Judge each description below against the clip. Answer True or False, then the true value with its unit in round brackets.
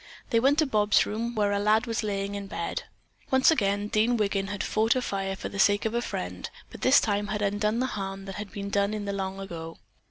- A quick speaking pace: True (245 wpm)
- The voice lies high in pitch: True (205 Hz)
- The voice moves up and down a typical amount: False (2.0 semitones)